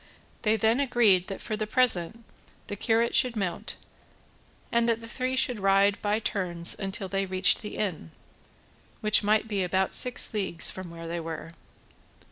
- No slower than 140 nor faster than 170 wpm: Yes, average, 165 wpm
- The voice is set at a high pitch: Yes, high, 205 Hz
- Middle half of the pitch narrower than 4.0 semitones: Yes, average, 3.4 semitones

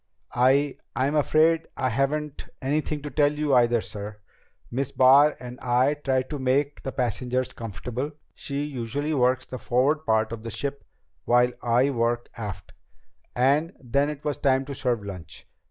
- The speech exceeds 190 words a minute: No, average, 160 wpm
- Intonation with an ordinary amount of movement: Yes, average, 3.1 semitones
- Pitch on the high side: No, low, 130 Hz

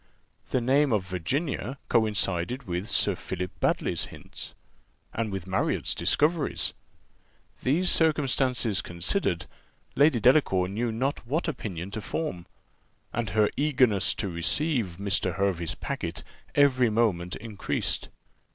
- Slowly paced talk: Yes, slow, 115 wpm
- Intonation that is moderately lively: No, wide, 6.4 semitones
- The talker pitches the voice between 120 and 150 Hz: No, low, 110 Hz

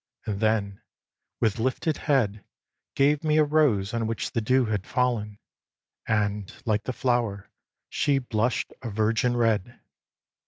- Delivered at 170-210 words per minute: No, slow, 135 wpm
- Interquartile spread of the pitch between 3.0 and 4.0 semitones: Yes, average, 3.5 semitones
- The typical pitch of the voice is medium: No, low, 115 Hz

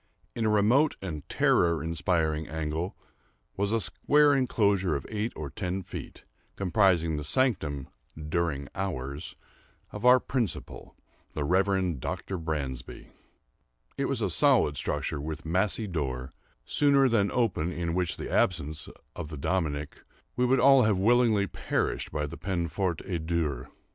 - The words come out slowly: No, average, 145 wpm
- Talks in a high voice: No, very low, 90 Hz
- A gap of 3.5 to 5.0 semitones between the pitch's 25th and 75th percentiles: No, wide, 5.4 semitones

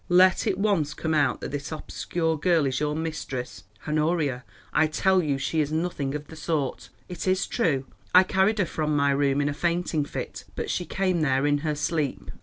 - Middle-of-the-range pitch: Yes, medium, 155 Hz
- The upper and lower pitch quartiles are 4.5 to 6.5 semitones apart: No, average, 3.5 semitones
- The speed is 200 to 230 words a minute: Yes, fast, 205 wpm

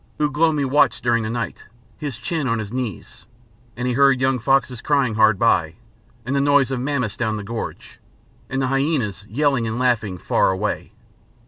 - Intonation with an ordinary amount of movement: Yes, average, 3.9 semitones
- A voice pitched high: No, low, 125 Hz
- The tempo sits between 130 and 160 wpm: No, average, 185 wpm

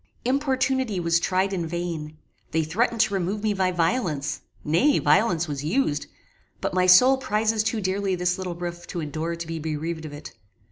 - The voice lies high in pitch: No, medium, 180 Hz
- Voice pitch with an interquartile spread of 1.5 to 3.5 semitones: No, average, 4.8 semitones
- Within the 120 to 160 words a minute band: No, average, 180 wpm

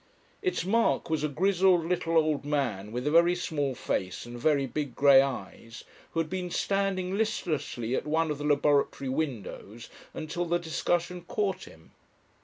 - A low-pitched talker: No, medium, 155 Hz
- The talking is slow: No, average, 165 wpm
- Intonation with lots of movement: No, average, 4.5 semitones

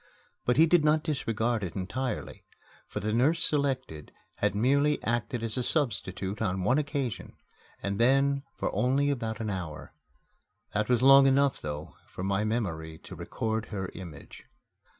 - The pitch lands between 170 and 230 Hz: No, low, 115 Hz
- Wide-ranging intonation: Yes, wide, 5.7 semitones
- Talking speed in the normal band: Yes, average, 155 wpm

